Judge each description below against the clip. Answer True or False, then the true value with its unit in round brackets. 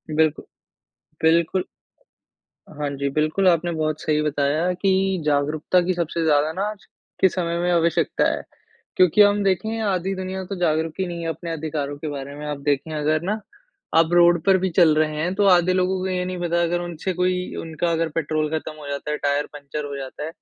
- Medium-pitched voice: True (165 Hz)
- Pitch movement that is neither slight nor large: True (3.1 semitones)